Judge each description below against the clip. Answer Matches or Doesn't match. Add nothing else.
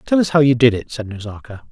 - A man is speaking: Matches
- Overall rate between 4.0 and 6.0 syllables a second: Doesn't match